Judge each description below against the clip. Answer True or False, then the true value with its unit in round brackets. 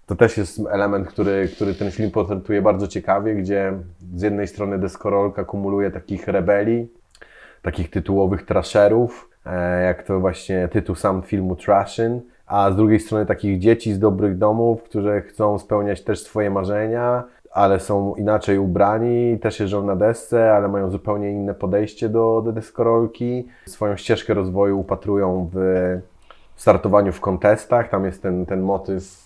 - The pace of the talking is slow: False (150 wpm)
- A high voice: False (100 Hz)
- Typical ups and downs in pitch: False (1.9 semitones)